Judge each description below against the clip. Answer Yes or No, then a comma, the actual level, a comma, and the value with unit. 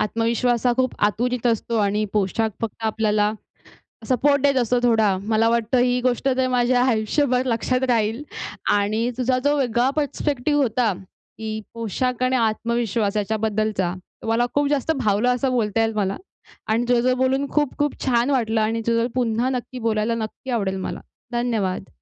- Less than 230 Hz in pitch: No, high, 235 Hz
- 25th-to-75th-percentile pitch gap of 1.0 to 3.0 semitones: Yes, narrow, 2.6 semitones